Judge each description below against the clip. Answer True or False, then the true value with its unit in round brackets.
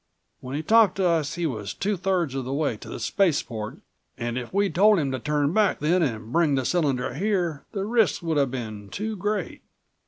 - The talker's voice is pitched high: False (155 Hz)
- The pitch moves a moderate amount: False (6.8 semitones)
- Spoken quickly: True (215 wpm)